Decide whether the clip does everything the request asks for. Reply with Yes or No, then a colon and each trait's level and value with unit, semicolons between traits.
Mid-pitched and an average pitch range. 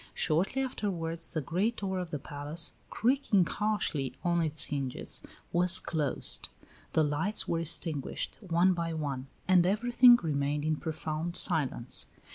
Yes: medium, 165 Hz; average, 3.9 semitones